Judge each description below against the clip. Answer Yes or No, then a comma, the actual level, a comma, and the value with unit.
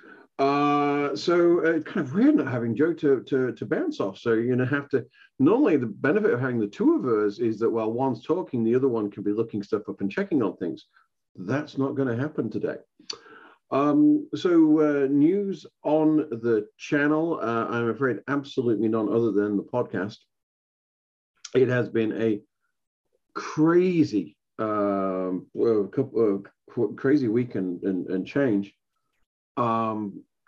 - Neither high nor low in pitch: No, low, 125 Hz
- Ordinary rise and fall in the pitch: No, wide, 5.7 semitones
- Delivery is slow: No, average, 160 wpm